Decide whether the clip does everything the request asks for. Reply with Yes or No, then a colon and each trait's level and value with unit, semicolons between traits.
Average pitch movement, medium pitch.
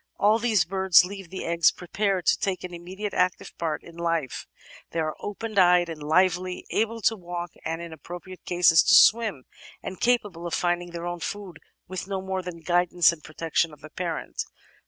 No: narrow, 2.2 semitones; medium, 175 Hz